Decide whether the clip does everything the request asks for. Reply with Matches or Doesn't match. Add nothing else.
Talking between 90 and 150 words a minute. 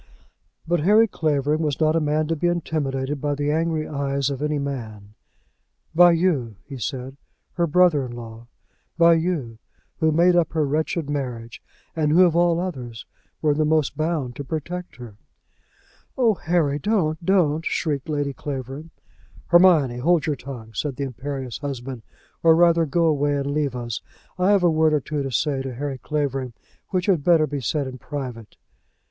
Doesn't match